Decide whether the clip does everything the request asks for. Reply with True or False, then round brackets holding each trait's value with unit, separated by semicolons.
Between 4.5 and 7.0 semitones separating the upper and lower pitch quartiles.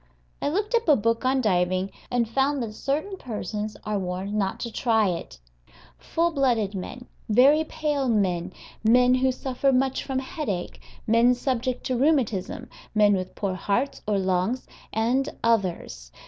True (5.0 semitones)